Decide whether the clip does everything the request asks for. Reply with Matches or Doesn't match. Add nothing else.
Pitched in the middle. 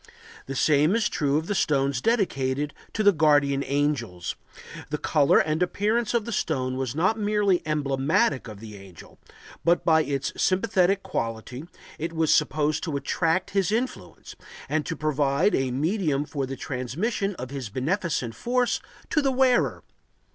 Matches